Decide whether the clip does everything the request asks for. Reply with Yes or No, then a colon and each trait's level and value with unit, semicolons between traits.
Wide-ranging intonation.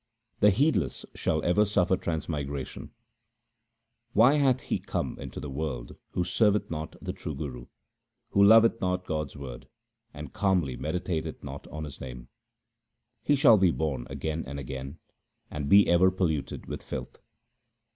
Yes: wide, 6.2 semitones